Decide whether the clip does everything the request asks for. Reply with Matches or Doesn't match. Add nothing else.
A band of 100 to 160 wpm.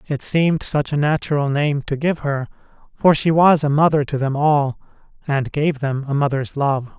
Doesn't match